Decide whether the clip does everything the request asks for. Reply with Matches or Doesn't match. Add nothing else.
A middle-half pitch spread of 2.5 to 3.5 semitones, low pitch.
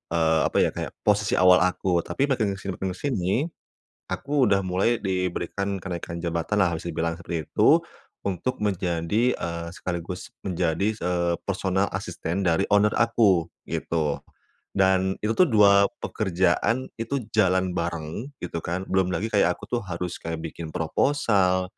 Matches